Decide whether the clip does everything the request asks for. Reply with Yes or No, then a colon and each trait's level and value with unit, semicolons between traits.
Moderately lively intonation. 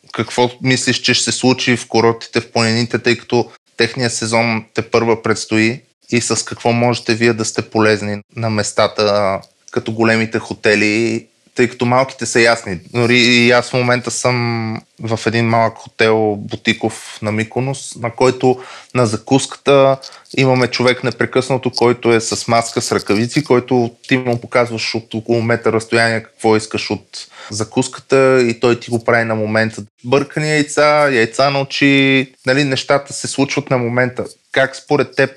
No: narrow, 2.1 semitones